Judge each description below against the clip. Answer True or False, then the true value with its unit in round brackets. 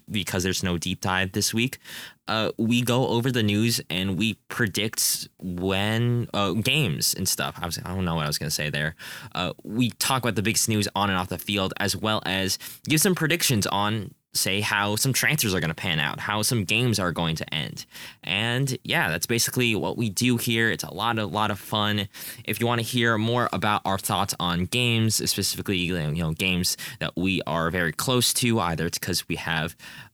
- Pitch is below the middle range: True (105 Hz)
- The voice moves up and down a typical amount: True (4.3 semitones)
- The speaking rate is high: True (215 wpm)